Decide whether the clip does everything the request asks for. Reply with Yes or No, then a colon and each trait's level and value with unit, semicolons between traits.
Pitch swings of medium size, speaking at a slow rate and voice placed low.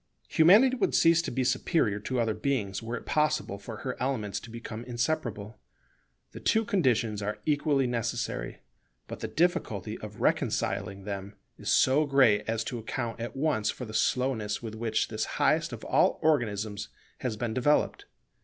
No: average, 4.4 semitones; average, 165 wpm; low, 120 Hz